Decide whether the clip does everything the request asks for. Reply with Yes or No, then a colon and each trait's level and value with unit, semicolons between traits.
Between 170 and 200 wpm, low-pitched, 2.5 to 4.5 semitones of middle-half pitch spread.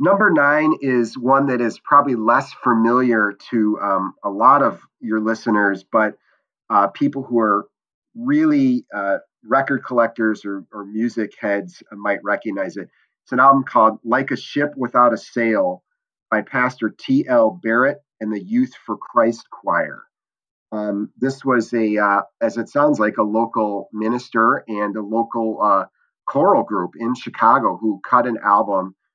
No: average, 155 wpm; low, 120 Hz; average, 4.1 semitones